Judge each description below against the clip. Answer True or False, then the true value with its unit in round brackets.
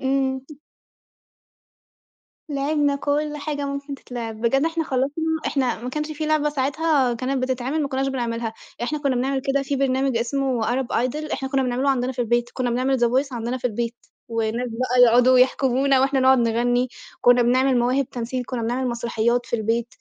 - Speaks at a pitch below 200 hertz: False (255 Hz)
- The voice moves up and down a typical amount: False (2.3 semitones)